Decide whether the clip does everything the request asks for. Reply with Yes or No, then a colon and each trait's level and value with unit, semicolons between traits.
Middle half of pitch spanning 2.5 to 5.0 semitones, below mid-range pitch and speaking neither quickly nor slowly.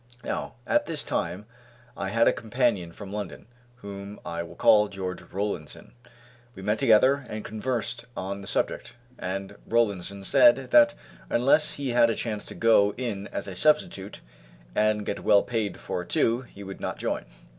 Yes: average, 3.5 semitones; low, 105 Hz; average, 170 wpm